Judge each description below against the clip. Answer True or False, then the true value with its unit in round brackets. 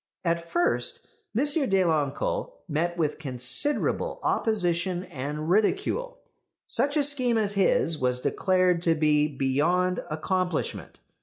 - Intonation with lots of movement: True (6.2 semitones)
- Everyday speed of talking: False (110 wpm)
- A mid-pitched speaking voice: True (175 Hz)